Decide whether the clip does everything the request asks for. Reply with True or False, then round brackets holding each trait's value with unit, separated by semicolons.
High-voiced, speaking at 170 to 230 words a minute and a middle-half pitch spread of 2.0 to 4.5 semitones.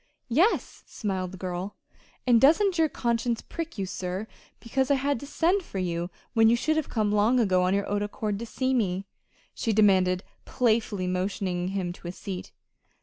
False (210 Hz; 185 wpm; 5.3 semitones)